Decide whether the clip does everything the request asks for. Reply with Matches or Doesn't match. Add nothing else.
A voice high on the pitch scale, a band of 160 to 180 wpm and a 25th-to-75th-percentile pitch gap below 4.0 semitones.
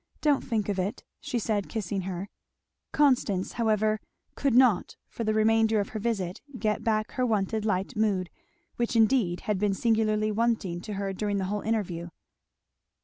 Matches